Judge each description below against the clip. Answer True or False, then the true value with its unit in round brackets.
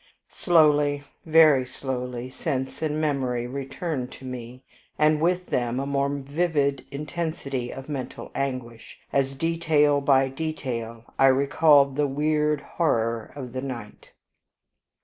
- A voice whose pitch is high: False (140 Hz)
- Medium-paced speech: False (125 wpm)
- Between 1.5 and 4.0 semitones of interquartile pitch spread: True (2.8 semitones)